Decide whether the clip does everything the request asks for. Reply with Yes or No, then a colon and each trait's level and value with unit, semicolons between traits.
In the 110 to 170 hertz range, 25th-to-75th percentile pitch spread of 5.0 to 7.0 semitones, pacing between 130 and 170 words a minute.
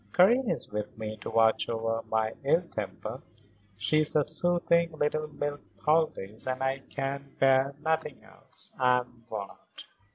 Yes: low, 135 Hz; wide, 5.4 semitones; average, 160 wpm